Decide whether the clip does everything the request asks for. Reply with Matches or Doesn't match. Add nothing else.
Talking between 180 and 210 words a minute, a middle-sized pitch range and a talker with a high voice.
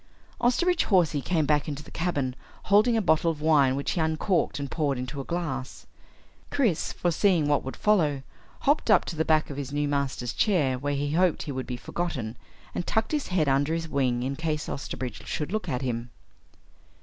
Doesn't match